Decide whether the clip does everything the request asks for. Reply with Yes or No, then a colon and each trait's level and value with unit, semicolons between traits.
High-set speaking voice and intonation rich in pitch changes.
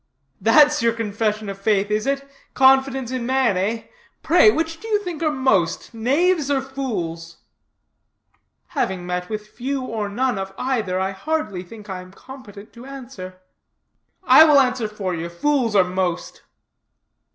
Yes: high, 225 Hz; wide, 5.7 semitones